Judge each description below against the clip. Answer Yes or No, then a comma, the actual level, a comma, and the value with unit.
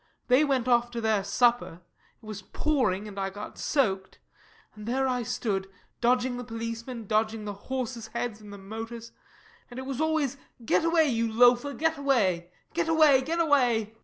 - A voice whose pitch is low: No, high, 240 Hz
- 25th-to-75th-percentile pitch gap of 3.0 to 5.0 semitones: Yes, average, 3.7 semitones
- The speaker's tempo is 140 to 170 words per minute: No, average, 180 wpm